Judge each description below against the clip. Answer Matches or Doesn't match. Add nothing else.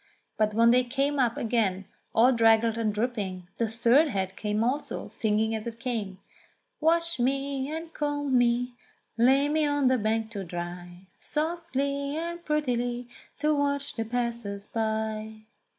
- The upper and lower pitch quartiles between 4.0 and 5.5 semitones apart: Matches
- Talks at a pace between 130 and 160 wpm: Matches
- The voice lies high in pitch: Matches